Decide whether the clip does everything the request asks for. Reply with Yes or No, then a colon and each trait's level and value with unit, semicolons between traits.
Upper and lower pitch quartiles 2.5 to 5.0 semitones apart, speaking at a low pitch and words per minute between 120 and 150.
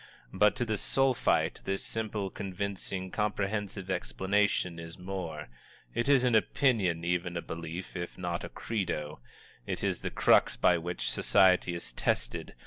Yes: average, 3.3 semitones; very low, 95 Hz; average, 145 wpm